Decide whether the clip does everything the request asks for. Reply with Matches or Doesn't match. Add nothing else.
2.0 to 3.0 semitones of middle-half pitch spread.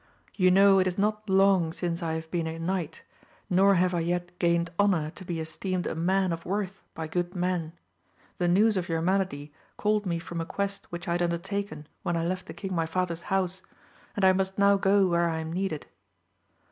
Matches